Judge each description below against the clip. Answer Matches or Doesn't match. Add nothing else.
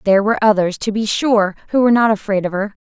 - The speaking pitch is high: Matches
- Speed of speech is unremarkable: Doesn't match